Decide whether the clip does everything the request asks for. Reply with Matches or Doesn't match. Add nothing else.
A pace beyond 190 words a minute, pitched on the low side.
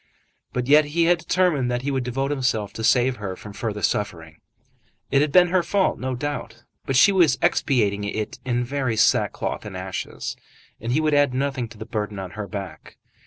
Matches